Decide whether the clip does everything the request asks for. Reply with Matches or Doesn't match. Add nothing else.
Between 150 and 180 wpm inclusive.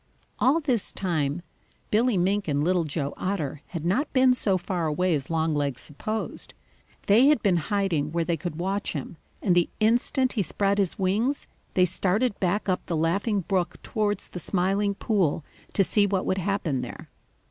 Matches